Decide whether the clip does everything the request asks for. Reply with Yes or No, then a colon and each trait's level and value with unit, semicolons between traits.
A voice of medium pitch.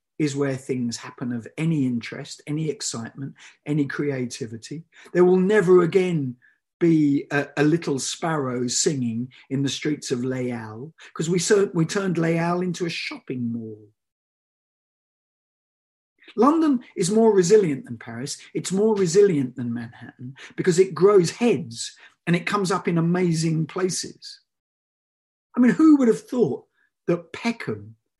Yes: medium, 160 Hz